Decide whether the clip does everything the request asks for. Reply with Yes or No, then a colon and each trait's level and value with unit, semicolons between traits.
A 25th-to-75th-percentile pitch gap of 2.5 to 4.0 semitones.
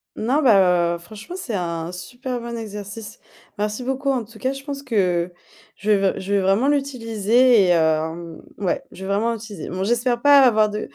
No: average, 4.8 semitones